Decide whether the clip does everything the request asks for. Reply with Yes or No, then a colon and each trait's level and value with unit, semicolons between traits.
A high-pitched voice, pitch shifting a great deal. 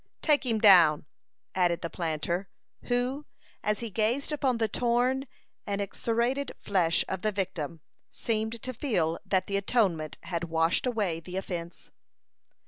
Yes: high, 200 Hz; wide, 5.7 semitones